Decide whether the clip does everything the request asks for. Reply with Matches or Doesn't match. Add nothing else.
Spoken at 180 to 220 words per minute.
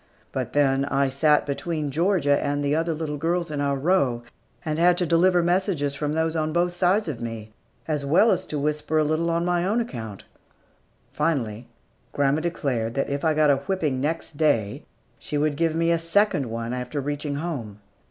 Matches